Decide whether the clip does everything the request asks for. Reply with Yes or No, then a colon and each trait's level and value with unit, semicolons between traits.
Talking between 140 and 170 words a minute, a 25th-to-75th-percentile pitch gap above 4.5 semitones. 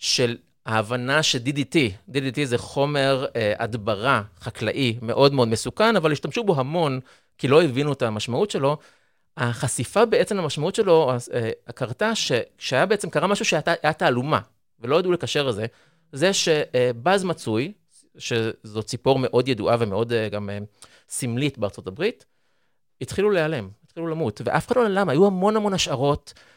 Yes: fast, 150 wpm; wide, 5.5 semitones